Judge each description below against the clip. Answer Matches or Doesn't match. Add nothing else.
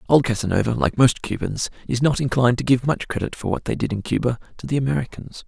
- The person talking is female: Doesn't match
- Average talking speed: Doesn't match